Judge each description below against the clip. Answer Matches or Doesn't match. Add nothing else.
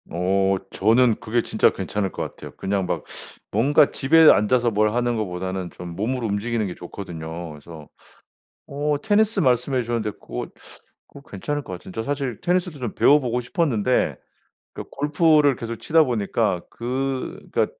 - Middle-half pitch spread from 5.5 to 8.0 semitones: Matches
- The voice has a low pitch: Matches